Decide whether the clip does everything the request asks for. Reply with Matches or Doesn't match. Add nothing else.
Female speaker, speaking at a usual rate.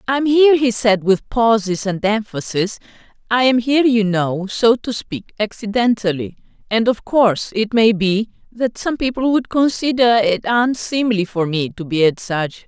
Matches